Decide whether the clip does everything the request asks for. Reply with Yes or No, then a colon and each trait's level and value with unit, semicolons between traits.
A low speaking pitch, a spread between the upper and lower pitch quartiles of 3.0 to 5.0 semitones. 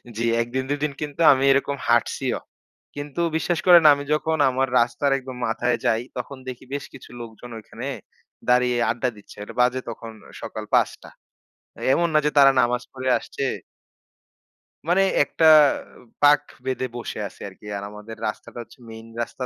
Yes: low, 130 Hz; average, 3.3 semitones